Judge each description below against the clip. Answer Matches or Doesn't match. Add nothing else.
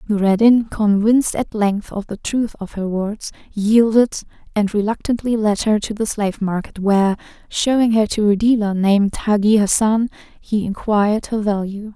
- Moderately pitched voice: Doesn't match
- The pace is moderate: Matches